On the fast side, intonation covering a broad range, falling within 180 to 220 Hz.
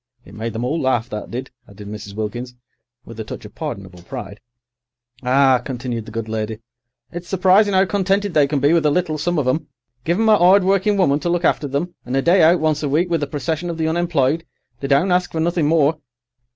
No: fast, 230 wpm; wide, 6.0 semitones; medium, 150 Hz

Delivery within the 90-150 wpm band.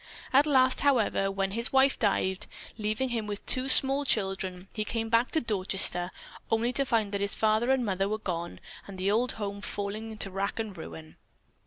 No: average, 190 wpm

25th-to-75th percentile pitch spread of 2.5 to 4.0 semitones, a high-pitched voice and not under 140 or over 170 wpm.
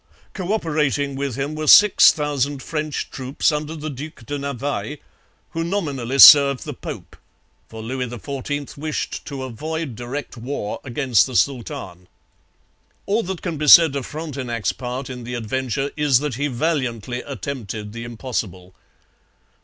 No: average, 3.5 semitones; medium, 140 Hz; average, 145 wpm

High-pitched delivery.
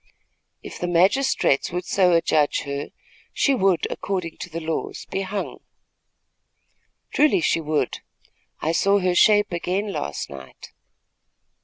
No: medium, 180 Hz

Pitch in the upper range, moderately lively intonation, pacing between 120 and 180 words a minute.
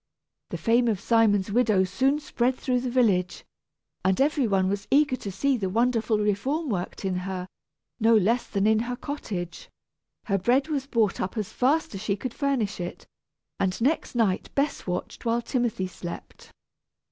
Yes: high, 225 Hz; average, 4.7 semitones; average, 170 wpm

